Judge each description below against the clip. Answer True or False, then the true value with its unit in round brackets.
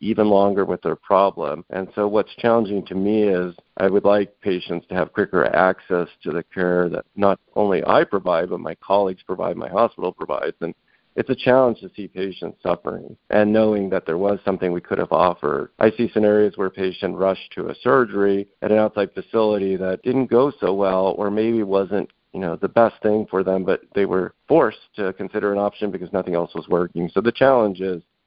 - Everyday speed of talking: False (210 wpm)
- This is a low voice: True (100 Hz)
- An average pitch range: False (2.2 semitones)